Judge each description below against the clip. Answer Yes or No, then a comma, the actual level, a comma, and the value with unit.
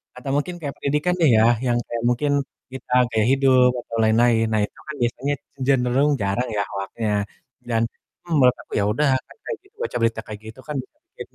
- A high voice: No, low, 125 Hz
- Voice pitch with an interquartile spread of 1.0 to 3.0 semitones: No, average, 4.0 semitones